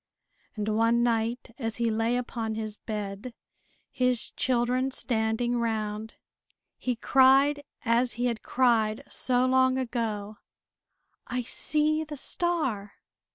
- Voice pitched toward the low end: No, high, 235 Hz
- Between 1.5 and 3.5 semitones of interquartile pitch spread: Yes, narrow, 2.5 semitones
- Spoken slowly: Yes, slow, 115 wpm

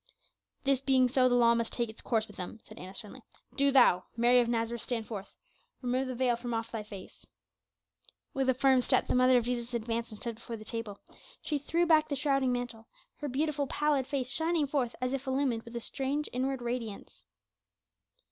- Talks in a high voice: Yes, very high, 250 Hz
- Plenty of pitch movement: No, average, 2.8 semitones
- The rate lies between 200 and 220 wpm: Yes, fast, 205 wpm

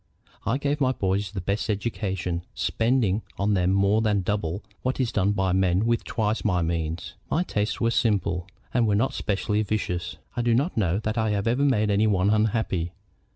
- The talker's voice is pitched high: No, low, 105 Hz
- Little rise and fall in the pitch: No, average, 3.2 semitones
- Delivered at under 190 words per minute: No, average, 200 wpm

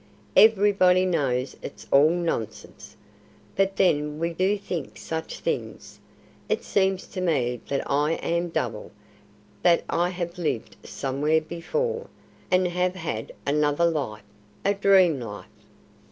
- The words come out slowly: Yes, slow, 125 wpm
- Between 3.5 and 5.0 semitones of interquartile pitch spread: Yes, average, 4.4 semitones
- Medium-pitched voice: Yes, medium, 170 Hz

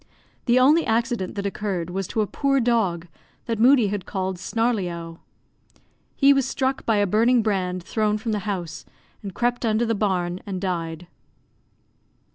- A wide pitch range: No, average, 4.4 semitones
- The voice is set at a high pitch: Yes, high, 210 Hz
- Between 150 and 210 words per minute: Yes, average, 160 wpm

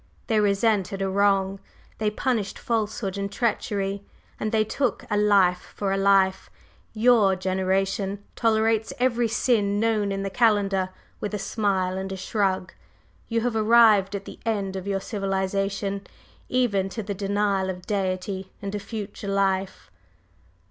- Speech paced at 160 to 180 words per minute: No, average, 150 wpm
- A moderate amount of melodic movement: No, narrow, 1.9 semitones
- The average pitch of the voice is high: Yes, high, 200 Hz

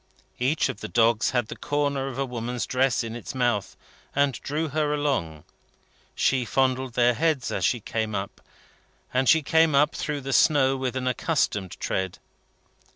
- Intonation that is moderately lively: Yes, average, 3.3 semitones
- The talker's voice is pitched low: Yes, low, 130 Hz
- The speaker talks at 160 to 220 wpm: Yes, average, 170 wpm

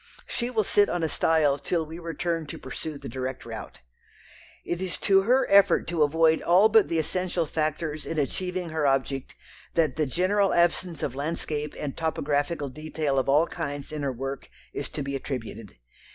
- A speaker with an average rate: Yes, average, 180 wpm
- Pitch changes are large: No, average, 3.5 semitones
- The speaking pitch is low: No, medium, 155 Hz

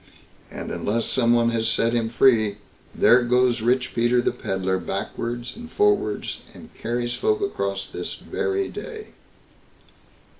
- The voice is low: Yes, low, 120 Hz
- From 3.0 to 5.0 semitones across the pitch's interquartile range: No, narrow, 2.6 semitones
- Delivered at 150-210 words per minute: No, average, 140 wpm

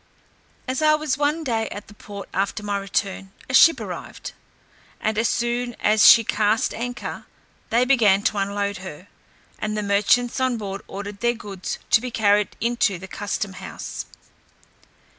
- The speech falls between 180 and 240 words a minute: No, average, 160 wpm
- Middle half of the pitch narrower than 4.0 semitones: Yes, average, 3.1 semitones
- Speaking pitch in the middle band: No, high, 210 Hz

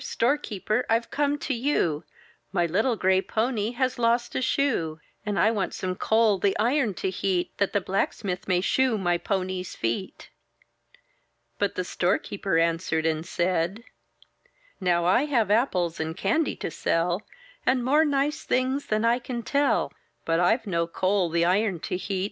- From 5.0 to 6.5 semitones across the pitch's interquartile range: Yes, wide, 5.4 semitones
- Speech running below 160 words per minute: No, average, 165 wpm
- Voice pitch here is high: Yes, high, 200 Hz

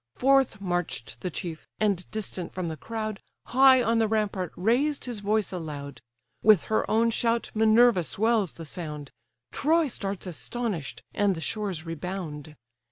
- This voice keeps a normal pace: Yes, average, 150 wpm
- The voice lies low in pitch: No, high, 205 Hz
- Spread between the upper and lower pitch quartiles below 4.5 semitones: No, average, 4.8 semitones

